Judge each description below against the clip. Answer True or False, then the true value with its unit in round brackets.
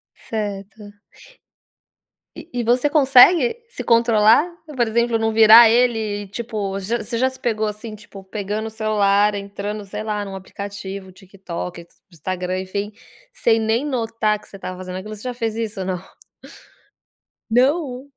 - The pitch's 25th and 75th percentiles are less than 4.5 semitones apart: True (3.0 semitones)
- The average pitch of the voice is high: True (215 Hz)